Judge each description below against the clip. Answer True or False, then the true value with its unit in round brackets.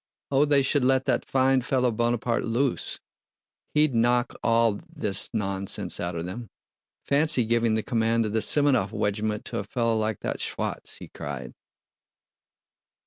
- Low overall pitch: True (115 Hz)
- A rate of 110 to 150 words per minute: True (145 wpm)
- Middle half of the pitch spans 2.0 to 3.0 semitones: False (3.4 semitones)